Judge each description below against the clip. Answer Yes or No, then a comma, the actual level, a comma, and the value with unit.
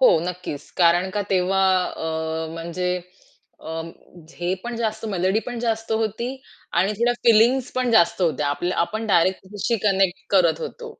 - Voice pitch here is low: No, high, 190 Hz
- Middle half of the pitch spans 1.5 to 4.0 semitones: No, average, 4.5 semitones